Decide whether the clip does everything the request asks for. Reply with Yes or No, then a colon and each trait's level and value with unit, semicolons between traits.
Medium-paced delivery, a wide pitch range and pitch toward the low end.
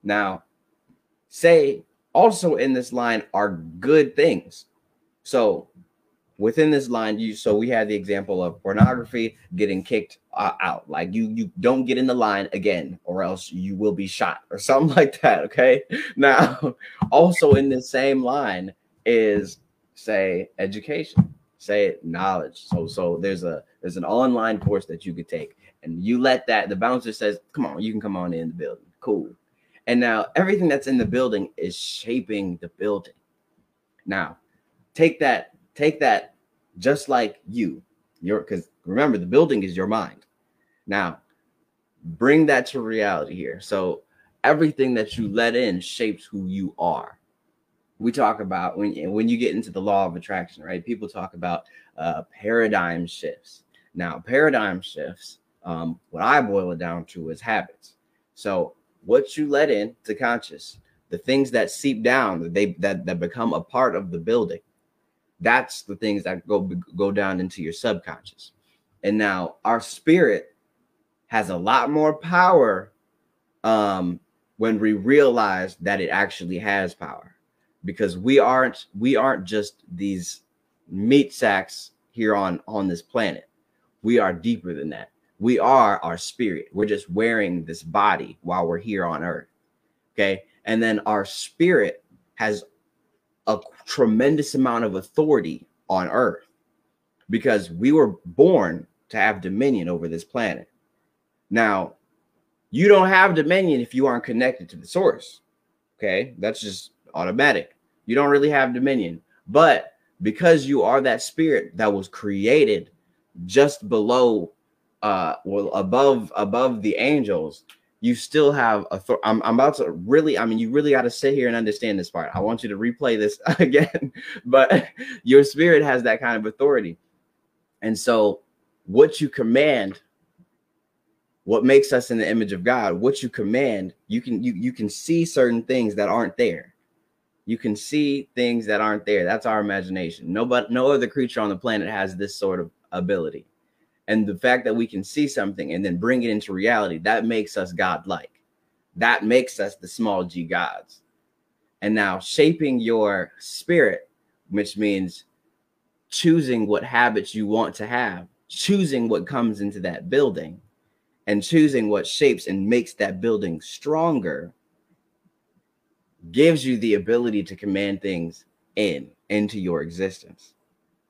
Yes: average, 160 wpm; wide, 5.9 semitones; low, 110 Hz